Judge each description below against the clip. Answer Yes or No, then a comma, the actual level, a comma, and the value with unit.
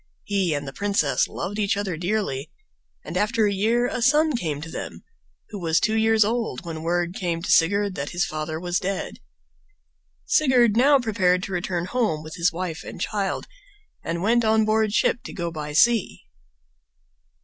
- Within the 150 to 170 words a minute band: No, average, 180 wpm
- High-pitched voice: Yes, high, 195 Hz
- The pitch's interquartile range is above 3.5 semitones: Yes, average, 4.6 semitones